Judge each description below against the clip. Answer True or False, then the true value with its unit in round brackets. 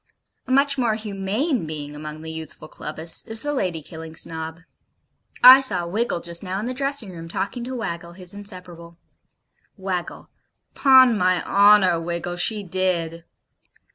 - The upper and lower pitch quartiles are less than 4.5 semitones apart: False (5.0 semitones)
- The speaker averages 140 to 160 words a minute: True (150 wpm)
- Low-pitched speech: False (185 Hz)